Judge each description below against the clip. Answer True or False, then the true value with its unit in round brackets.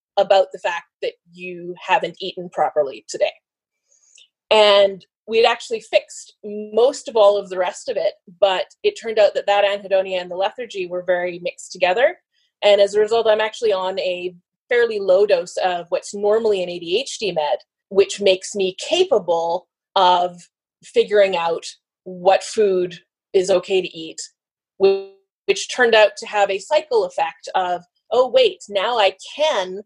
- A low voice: False (200 Hz)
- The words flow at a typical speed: True (160 wpm)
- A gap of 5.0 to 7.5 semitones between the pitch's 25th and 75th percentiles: True (5.5 semitones)